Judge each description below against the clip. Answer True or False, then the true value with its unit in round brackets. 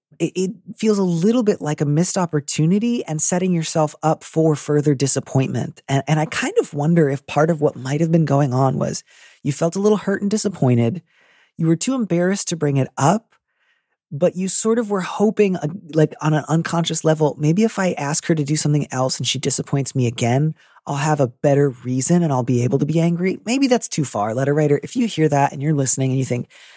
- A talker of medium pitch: True (155 Hz)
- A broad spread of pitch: False (4.7 semitones)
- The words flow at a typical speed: False (225 wpm)